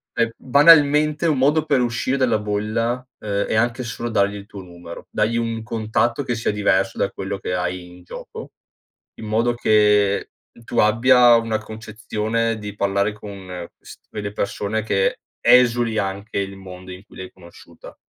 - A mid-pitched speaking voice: No, low, 110 Hz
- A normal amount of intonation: Yes, average, 3.0 semitones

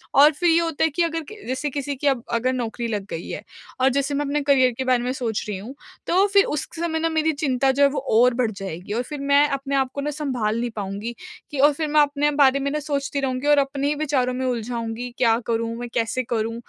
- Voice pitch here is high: Yes, very high, 270 Hz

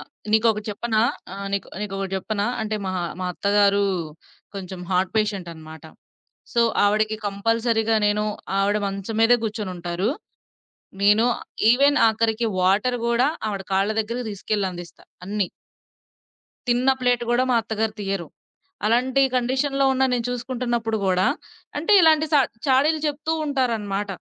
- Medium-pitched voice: No, high, 215 Hz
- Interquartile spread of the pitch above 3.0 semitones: Yes, average, 3.6 semitones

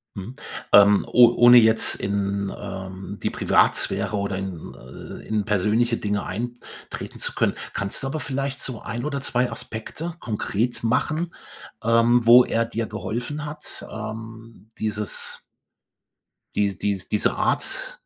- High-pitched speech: No, low, 110 Hz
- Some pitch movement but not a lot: Yes, average, 3.1 semitones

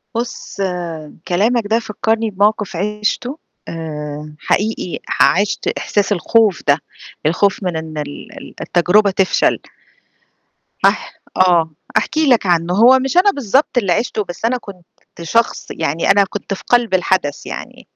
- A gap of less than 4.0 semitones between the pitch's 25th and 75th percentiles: No, average, 4.7 semitones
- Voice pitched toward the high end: Yes, high, 200 Hz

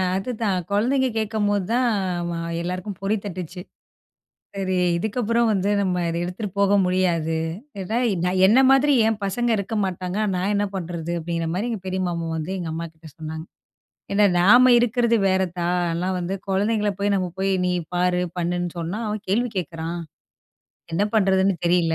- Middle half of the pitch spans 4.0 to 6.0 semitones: No, average, 3.1 semitones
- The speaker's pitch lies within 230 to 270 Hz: No, high, 190 Hz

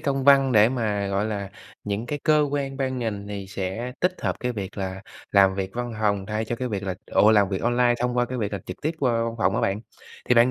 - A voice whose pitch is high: No, low, 110 Hz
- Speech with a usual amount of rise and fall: Yes, average, 3.8 semitones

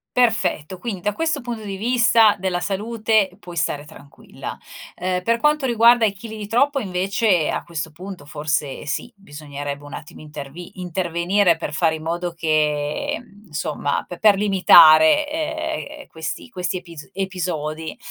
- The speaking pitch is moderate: Yes, medium, 180 Hz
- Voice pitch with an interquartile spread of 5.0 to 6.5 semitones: Yes, wide, 5.6 semitones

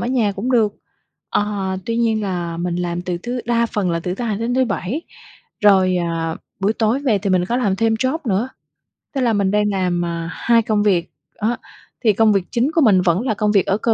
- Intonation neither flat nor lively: Yes, average, 4.1 semitones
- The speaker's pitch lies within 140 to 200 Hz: No, high, 210 Hz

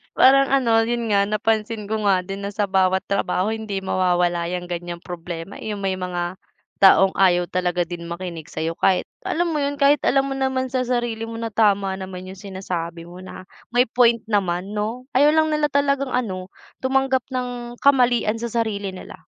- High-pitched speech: Yes, high, 200 Hz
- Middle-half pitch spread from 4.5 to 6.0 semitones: Yes, average, 4.8 semitones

